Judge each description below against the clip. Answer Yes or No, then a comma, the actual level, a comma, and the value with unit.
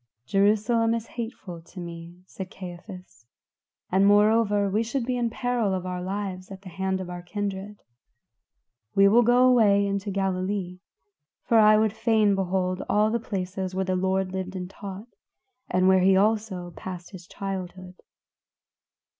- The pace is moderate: Yes, average, 155 wpm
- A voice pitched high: Yes, high, 195 Hz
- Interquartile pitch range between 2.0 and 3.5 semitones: Yes, narrow, 2.6 semitones